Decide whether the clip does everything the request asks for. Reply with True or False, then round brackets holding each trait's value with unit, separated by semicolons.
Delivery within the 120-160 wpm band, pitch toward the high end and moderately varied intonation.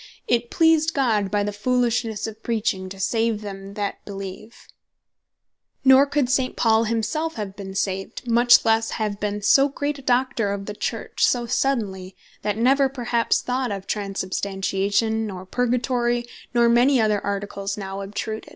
True (155 wpm; 220 Hz; 3.6 semitones)